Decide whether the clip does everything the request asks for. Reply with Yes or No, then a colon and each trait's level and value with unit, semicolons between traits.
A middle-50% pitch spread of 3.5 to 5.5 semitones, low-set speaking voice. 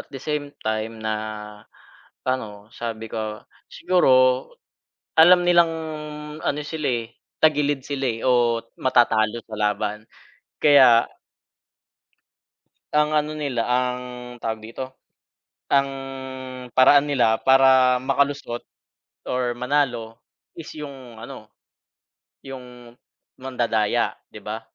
Yes: average, 3.9 semitones; low, 125 Hz